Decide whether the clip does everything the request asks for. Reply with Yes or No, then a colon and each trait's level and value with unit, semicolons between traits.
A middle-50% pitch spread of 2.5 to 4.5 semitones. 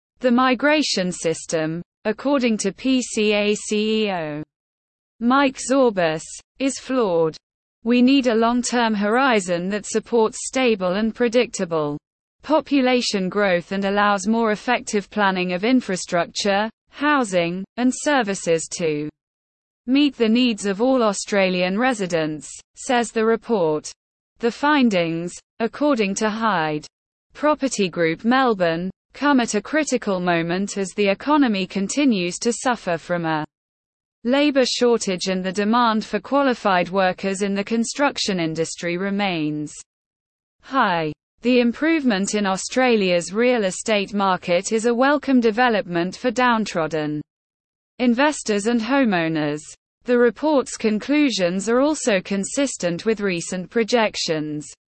No: wide, 5.6 semitones